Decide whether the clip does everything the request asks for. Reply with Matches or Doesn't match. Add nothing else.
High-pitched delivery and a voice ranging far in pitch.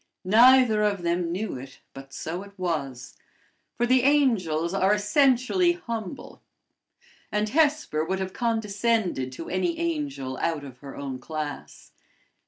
Matches